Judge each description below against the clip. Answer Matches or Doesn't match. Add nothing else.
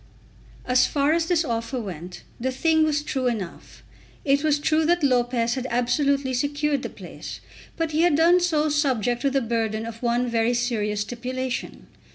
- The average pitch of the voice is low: Doesn't match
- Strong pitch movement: Doesn't match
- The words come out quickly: Doesn't match